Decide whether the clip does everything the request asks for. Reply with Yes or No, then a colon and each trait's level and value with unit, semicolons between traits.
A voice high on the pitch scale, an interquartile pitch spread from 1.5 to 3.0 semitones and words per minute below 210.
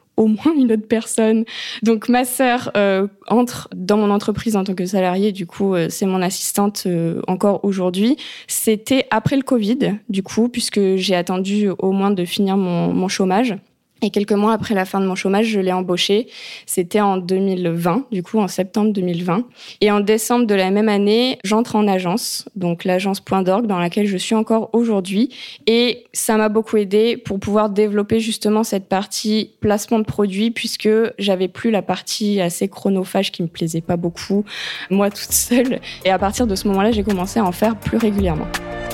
Yes: high, 205 Hz; average, 2.7 semitones; average, 190 wpm